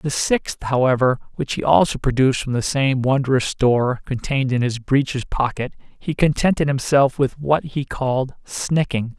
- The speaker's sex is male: Yes, male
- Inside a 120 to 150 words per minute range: No, average, 165 wpm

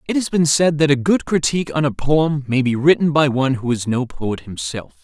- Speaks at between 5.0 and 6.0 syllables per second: Yes, 5.4 syllables/s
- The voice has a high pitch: No, medium, 140 Hz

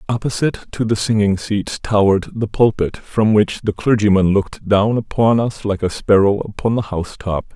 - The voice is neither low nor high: No, low, 105 Hz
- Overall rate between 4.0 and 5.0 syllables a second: No, 5.2 syllables/s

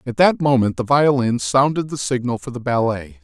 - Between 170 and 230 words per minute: Yes, fast, 205 wpm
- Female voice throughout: No, male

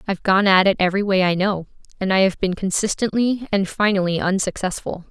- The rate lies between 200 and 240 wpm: No, average, 190 wpm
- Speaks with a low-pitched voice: No, high, 195 Hz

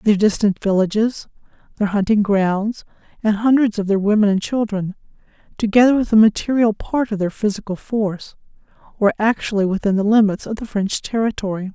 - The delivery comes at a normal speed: Yes, average, 160 wpm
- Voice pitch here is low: No, high, 210 Hz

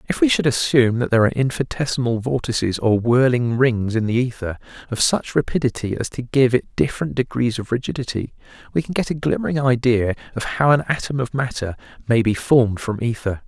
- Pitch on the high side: No, low, 125 Hz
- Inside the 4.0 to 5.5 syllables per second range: No, 6.0 syllables/s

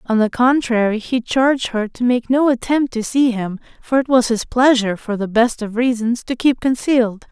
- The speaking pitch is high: Yes, high, 240 Hz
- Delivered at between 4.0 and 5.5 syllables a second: Yes, 5.0 syllables/s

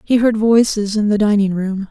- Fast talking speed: Yes, fast, 220 wpm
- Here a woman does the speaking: Yes, female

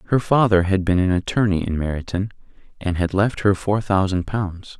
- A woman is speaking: No, male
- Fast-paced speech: No, average, 190 wpm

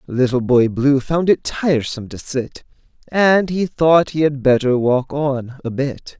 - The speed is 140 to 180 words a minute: Yes, average, 175 wpm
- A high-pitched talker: No, medium, 140 Hz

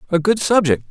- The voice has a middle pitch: Yes, medium, 180 Hz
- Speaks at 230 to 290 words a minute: No, average, 200 wpm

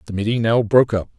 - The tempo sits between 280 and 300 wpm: No, fast, 255 wpm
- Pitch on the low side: Yes, low, 110 Hz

